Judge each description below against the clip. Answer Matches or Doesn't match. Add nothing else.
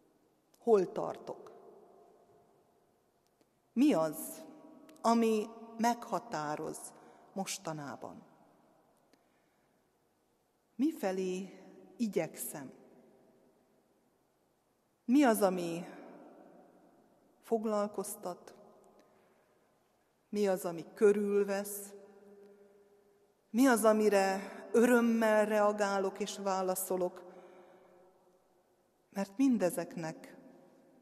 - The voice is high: Matches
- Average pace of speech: Doesn't match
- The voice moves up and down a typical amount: Matches